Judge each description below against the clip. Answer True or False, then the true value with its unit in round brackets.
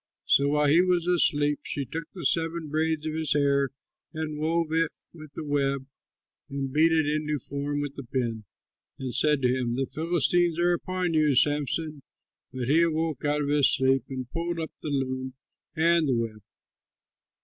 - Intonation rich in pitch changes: False (2.9 semitones)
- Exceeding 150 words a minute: True (180 wpm)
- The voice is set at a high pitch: False (150 Hz)